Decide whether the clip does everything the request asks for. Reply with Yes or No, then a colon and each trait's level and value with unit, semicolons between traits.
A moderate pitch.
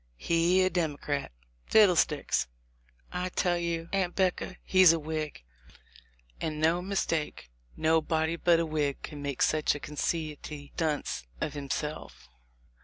Yes: medium, 160 Hz